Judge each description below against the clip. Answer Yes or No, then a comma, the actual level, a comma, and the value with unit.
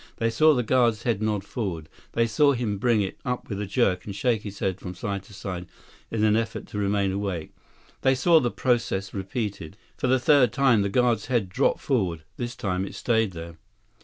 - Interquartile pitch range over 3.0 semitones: Yes, average, 3.9 semitones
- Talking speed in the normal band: No, fast, 210 wpm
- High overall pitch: No, low, 105 Hz